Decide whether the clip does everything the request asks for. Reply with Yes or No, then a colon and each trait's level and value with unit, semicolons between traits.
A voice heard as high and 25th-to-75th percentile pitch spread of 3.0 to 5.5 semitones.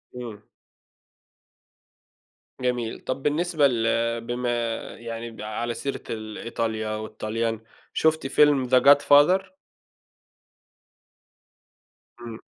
No: low, 120 Hz; average, 3.7 semitones